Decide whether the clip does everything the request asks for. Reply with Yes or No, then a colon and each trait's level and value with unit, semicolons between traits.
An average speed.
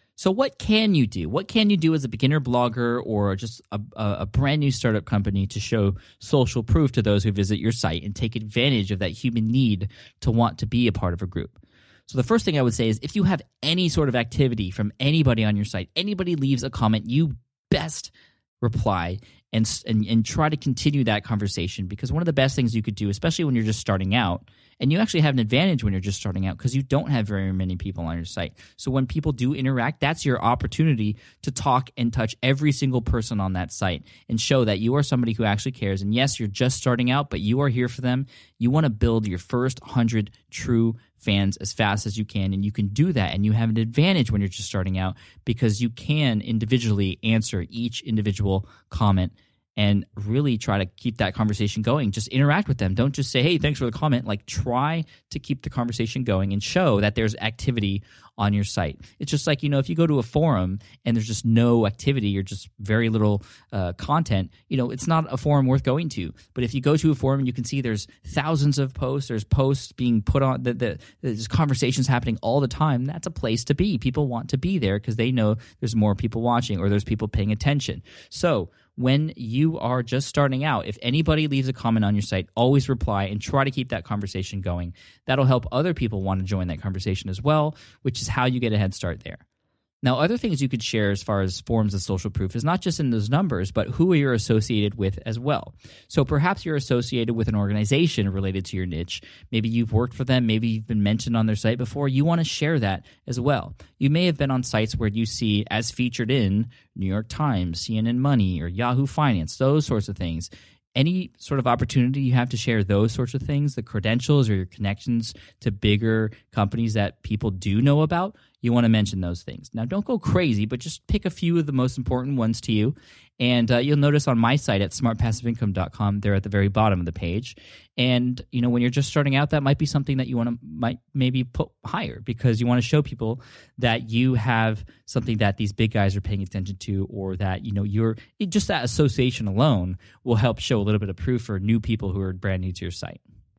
No: fast, 235 wpm